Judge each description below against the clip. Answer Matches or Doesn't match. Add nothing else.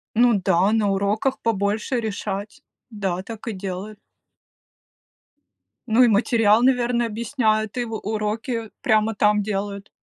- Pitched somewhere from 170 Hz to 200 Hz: Doesn't match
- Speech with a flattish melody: Matches